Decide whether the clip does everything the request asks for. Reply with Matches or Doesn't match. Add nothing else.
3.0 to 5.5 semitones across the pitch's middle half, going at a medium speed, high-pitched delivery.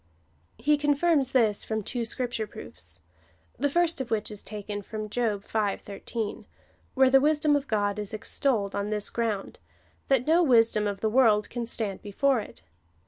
Matches